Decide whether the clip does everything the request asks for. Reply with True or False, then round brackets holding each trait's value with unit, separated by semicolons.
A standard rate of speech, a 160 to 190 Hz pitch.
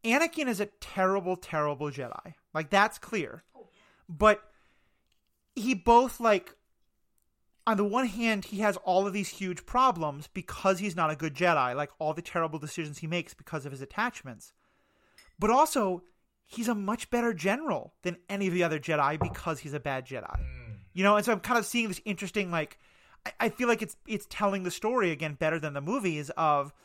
True (190 wpm; 185 Hz)